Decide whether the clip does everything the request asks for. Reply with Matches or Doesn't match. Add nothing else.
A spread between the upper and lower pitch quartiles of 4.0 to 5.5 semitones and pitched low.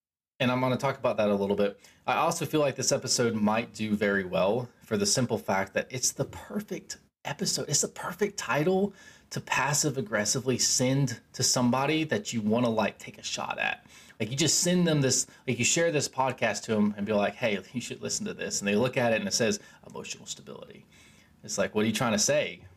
Matches